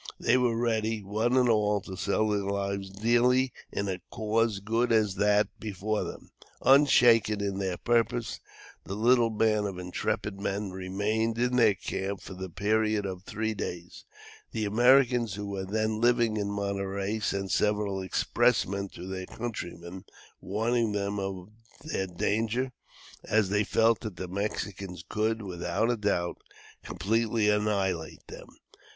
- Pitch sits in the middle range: No, low, 105 Hz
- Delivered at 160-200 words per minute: No, average, 145 wpm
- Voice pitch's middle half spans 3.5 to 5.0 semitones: No, narrow, 2.6 semitones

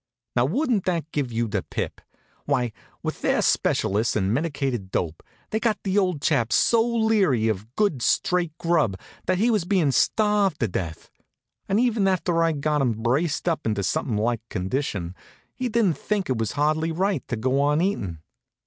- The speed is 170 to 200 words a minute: Yes, average, 175 wpm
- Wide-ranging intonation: Yes, wide, 8.8 semitones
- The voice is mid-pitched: Yes, medium, 150 Hz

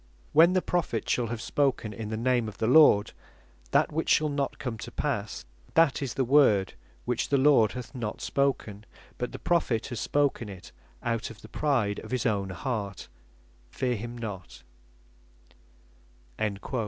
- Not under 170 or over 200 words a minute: No, average, 160 wpm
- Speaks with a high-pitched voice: No, low, 120 Hz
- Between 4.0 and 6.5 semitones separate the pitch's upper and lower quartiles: Yes, average, 4.4 semitones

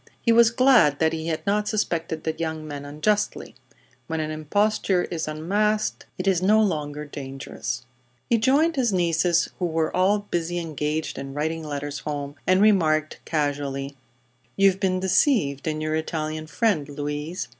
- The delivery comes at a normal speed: Yes, average, 155 wpm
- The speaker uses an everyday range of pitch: Yes, average, 4.9 semitones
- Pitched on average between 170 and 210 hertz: No, medium, 160 Hz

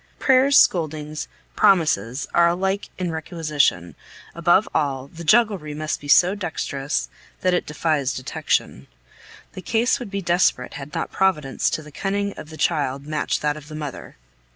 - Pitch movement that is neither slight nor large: Yes, average, 4.3 semitones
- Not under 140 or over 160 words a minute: Yes, average, 155 wpm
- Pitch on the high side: No, medium, 160 Hz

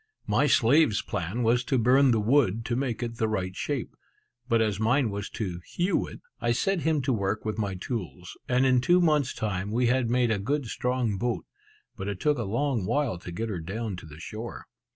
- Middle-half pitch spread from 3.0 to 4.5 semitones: Yes, average, 4.2 semitones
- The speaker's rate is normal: No, fast, 215 wpm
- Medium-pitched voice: No, low, 115 Hz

